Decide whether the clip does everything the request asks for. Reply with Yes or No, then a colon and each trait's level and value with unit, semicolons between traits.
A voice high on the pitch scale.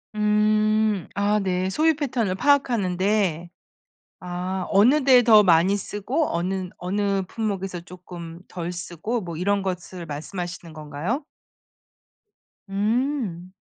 Yes: high, 195 Hz